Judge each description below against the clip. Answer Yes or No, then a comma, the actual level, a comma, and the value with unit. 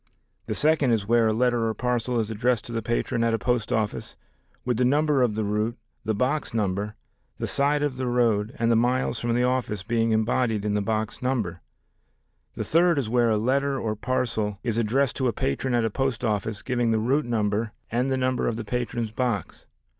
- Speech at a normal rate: No, fast, 215 wpm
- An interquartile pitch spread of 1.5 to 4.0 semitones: Yes, average, 2.7 semitones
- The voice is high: No, low, 115 Hz